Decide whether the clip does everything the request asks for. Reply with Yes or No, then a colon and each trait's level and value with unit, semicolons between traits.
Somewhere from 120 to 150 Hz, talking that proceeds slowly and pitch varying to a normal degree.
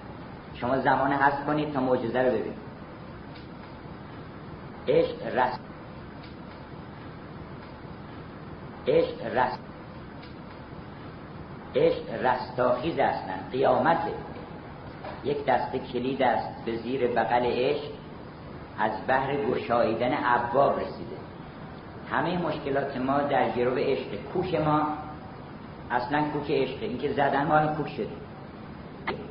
Yes: medium, 140 Hz; slow, 100 wpm; average, 3.5 semitones